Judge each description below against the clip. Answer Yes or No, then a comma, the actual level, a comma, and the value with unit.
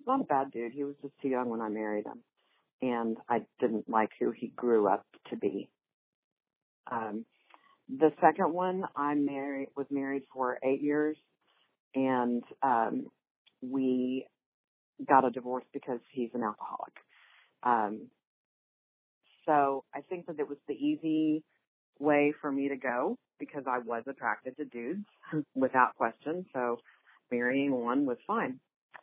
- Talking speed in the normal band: Yes, average, 145 wpm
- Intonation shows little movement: No, average, 3.3 semitones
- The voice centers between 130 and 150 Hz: Yes, medium, 140 Hz